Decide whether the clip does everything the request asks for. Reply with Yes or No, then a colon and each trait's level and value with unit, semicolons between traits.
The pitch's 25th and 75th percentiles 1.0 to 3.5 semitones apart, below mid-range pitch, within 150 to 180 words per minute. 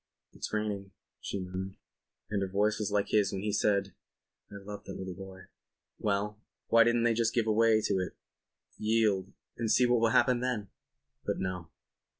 Yes: narrow, 2.6 semitones; low, 105 Hz; average, 170 wpm